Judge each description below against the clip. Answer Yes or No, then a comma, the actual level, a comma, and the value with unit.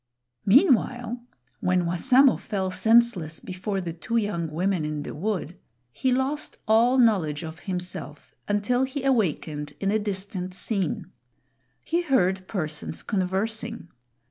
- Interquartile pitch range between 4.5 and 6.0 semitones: Yes, average, 5.1 semitones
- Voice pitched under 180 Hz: No, high, 195 Hz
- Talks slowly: Yes, slow, 125 wpm